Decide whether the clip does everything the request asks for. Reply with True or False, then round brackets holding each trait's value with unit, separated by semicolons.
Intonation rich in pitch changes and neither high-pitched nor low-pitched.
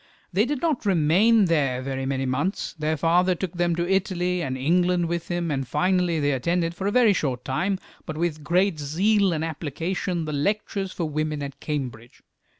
False (3.9 semitones; 170 Hz)